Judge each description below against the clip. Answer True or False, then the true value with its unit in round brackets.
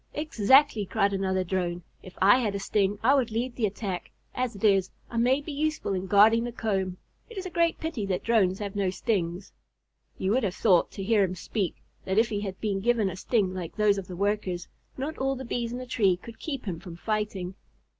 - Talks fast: True (225 wpm)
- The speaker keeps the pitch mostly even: False (4.0 semitones)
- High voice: True (205 Hz)